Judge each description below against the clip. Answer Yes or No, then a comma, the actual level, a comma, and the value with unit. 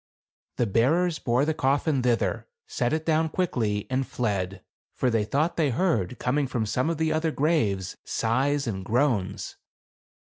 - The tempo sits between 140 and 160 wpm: Yes, average, 155 wpm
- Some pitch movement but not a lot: No, wide, 5.8 semitones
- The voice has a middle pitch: No, low, 130 Hz